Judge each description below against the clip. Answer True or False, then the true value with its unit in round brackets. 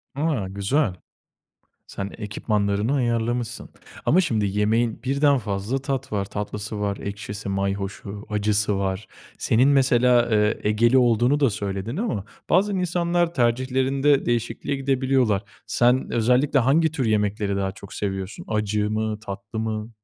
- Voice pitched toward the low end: True (110 Hz)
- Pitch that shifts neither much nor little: True (4.4 semitones)